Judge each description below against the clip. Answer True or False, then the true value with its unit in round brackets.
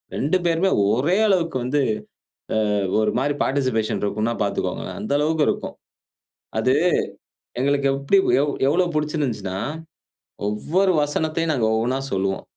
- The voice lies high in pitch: False (140 Hz)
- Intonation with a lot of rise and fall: True (6.0 semitones)